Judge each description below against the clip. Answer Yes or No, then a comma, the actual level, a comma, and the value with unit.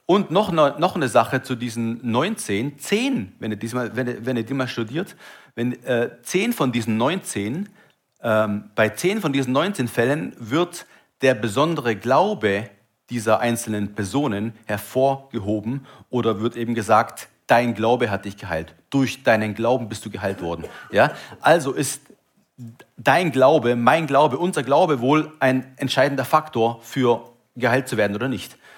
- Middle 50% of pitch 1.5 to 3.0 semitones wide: No, average, 3.6 semitones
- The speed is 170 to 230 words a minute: No, average, 155 wpm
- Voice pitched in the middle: No, low, 125 Hz